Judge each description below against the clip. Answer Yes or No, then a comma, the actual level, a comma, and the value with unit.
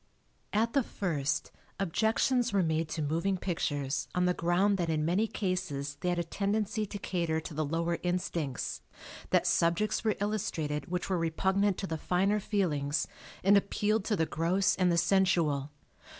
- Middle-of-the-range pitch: Yes, medium, 180 Hz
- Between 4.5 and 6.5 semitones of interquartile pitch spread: No, average, 3.8 semitones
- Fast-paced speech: No, average, 165 wpm